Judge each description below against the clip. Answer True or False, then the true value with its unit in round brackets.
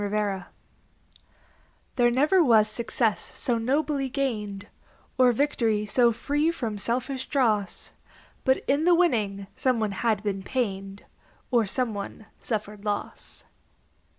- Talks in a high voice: True (230 Hz)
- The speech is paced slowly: True (125 wpm)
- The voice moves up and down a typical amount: True (4.1 semitones)